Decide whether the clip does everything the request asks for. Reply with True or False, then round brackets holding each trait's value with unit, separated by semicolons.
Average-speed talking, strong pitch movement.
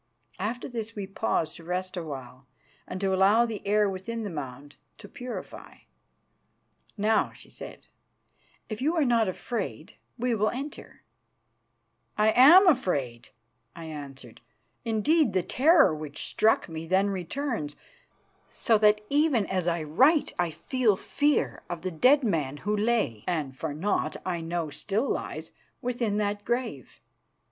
True (145 wpm; 6.5 semitones)